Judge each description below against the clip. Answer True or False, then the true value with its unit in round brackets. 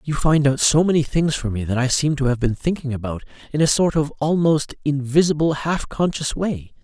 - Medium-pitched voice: True (145 Hz)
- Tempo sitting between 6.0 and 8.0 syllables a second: False (5.3 syllables/s)